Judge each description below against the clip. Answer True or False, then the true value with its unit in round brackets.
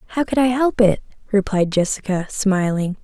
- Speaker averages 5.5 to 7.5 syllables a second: False (5.1 syllables/s)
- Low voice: False (205 Hz)